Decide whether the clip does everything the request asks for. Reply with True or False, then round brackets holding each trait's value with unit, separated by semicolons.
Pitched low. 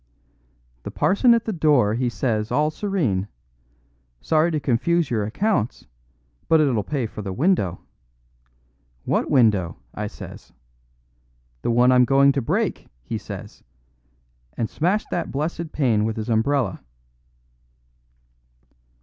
True (130 Hz)